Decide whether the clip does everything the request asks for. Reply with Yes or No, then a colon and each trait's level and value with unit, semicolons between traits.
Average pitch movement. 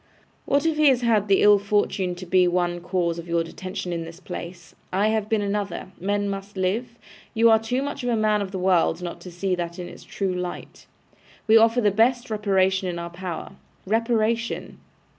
Yes: average, 3.7 semitones